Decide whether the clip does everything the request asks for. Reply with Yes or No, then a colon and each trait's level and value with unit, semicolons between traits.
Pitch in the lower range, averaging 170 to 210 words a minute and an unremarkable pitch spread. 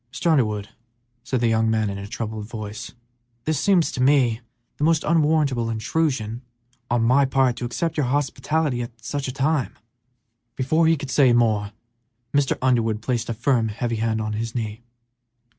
Yes: low, 120 Hz; average, 175 wpm; average, 4.0 semitones